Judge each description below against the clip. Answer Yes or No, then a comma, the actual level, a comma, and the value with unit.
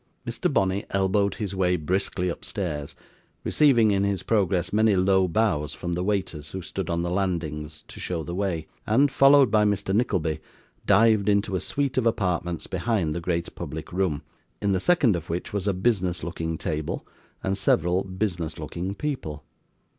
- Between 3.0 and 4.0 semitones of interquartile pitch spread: Yes, average, 3.3 semitones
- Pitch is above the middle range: No, very low, 95 Hz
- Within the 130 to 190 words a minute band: Yes, average, 170 wpm